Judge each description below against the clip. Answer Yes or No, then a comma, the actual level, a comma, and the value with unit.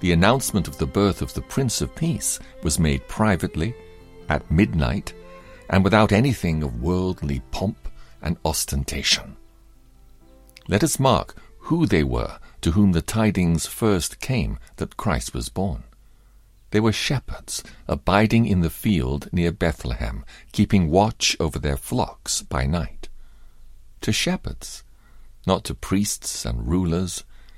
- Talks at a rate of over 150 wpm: No, slow, 135 wpm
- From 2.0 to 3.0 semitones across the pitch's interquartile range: No, wide, 5.5 semitones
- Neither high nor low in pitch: No, very low, 85 Hz